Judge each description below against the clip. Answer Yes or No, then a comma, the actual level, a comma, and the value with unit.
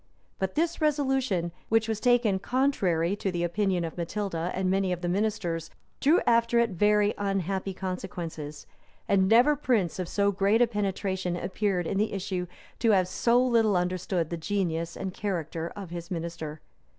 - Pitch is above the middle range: Yes, high, 195 Hz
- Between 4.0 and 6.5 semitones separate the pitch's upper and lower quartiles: No, average, 3.6 semitones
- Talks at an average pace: Yes, average, 165 wpm